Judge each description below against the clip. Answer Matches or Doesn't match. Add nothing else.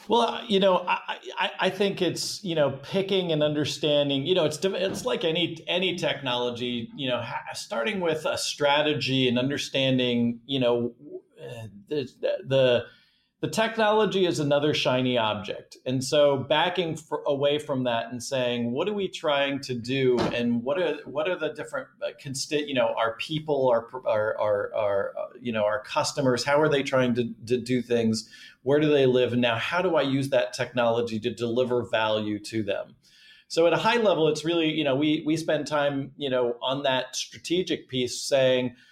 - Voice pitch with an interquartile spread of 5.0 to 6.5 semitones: Doesn't match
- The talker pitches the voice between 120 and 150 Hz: Matches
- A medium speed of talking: Matches